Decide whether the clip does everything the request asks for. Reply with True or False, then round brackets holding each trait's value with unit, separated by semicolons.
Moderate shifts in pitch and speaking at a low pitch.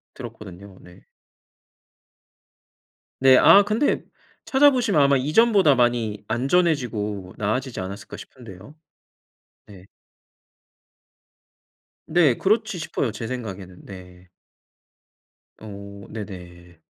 False (7.3 semitones; 115 Hz)